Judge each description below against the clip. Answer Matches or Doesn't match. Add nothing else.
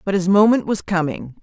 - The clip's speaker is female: Matches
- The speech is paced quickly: Matches